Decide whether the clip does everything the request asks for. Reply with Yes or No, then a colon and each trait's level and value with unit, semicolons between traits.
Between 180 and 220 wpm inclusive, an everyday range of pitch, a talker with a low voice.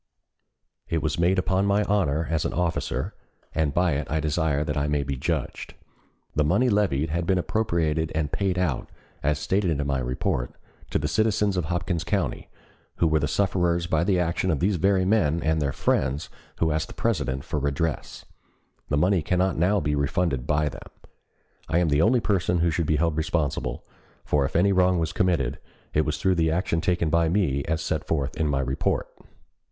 Yes: average, 195 wpm; average, 3.6 semitones; very low, 80 Hz